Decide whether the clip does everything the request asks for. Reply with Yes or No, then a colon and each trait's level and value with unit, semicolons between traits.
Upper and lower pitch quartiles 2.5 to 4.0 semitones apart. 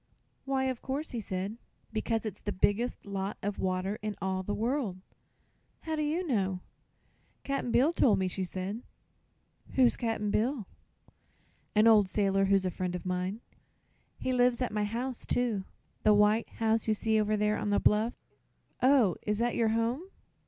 Yes: average, 3.7 semitones